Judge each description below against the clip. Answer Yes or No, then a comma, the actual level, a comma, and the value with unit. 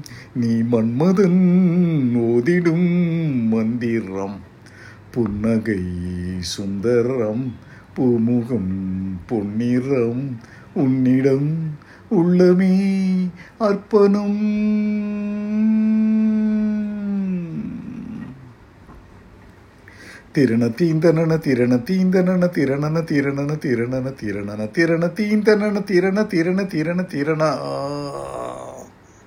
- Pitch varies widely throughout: Yes, wide, 8.6 semitones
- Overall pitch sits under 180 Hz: Yes, medium, 140 Hz